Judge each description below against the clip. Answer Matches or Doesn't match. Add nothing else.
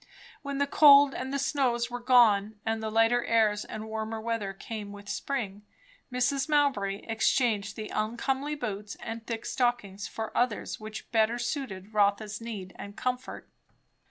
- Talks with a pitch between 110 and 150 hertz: Doesn't match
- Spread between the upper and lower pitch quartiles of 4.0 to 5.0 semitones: Doesn't match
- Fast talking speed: Doesn't match